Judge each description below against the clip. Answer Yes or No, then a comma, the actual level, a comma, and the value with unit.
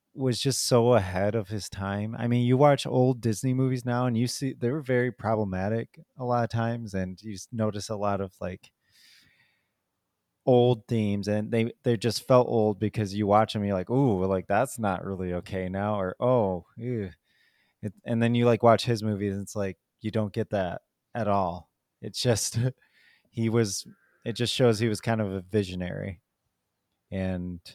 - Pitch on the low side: Yes, low, 110 Hz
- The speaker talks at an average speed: Yes, average, 190 wpm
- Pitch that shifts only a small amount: No, average, 3.3 semitones